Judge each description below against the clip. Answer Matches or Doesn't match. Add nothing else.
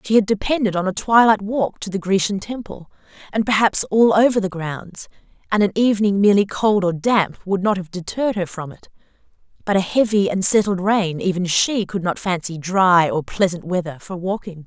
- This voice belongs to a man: Doesn't match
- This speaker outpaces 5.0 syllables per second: Matches